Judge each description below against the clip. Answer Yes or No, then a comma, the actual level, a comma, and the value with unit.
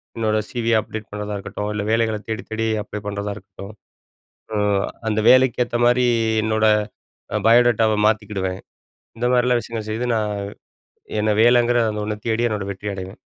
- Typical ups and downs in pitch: No, narrow, 2.0 semitones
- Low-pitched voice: Yes, low, 110 Hz